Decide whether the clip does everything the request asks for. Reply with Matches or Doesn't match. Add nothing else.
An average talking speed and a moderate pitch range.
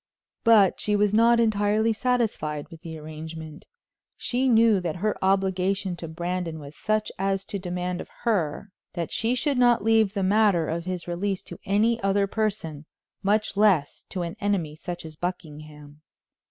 Matches